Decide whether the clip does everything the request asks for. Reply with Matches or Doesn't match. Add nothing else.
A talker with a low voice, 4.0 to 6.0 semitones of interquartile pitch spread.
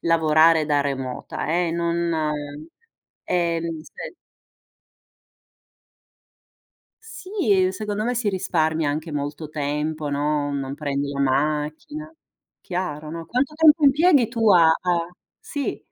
Doesn't match